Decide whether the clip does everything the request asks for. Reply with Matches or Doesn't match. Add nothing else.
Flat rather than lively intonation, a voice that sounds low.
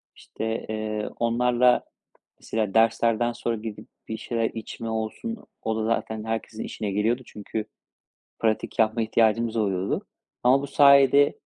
Matches